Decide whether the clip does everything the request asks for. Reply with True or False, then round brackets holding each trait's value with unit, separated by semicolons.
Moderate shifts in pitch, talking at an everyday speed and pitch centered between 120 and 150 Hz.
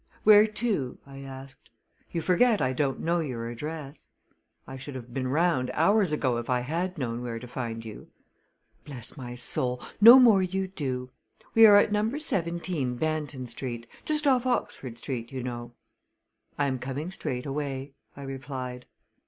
False (6.0 semitones; 160 wpm; 135 Hz)